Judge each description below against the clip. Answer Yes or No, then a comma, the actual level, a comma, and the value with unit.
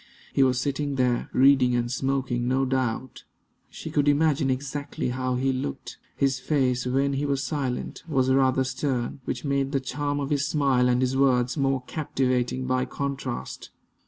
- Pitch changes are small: Yes, narrow, 1.6 semitones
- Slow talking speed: No, average, 165 wpm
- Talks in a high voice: No, low, 135 Hz